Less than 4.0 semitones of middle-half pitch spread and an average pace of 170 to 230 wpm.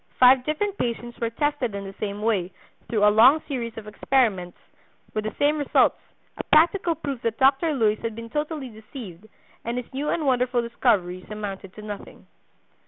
No: average, 4.7 semitones; average, 175 wpm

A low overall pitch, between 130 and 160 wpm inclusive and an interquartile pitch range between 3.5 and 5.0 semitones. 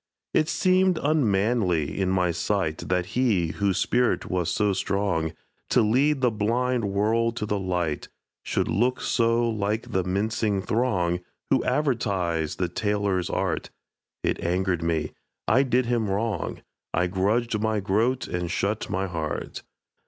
Yes: low, 100 Hz; average, 145 wpm; average, 4.4 semitones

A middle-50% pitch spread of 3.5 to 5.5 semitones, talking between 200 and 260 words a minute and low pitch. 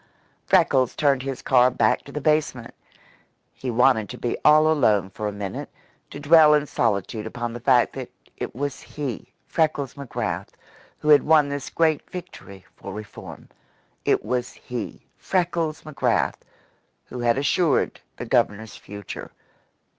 No: average, 4.6 semitones; average, 145 wpm; low, 130 Hz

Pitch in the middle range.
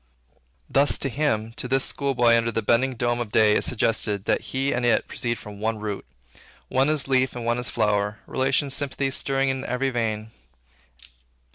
No: low, 120 Hz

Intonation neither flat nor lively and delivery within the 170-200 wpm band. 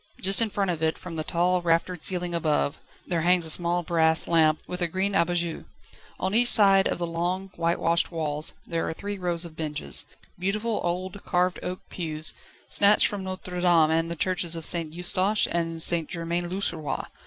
No: narrow, 2.0 semitones; average, 190 wpm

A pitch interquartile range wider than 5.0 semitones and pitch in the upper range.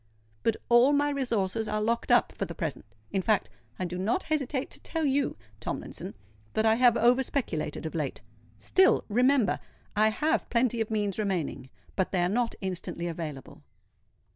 Yes: wide, 5.4 semitones; high, 220 Hz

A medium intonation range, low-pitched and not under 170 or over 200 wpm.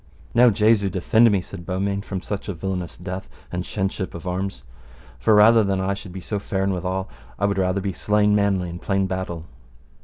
No: narrow, 1.7 semitones; very low, 95 Hz; average, 195 wpm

